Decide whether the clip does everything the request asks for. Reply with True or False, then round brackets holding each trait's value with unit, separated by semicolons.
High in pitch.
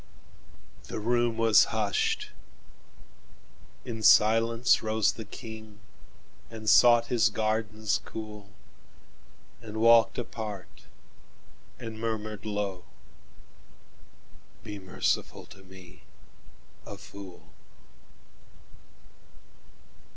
False (110 Hz)